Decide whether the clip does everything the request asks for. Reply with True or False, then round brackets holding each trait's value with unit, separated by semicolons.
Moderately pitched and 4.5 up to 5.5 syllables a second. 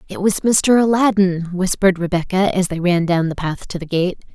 True (180 Hz; 5.2 syllables/s)